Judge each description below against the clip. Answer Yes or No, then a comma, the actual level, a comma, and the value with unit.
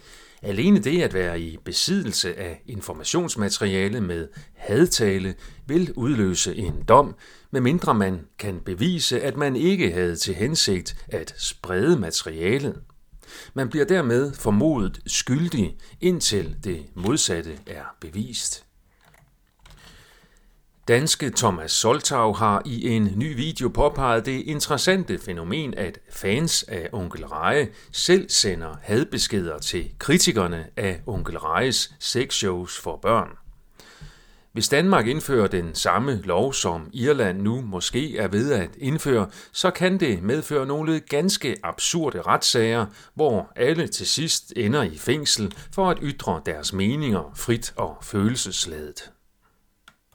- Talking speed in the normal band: No, slow, 120 wpm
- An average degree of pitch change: No, wide, 8.0 semitones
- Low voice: Yes, low, 120 Hz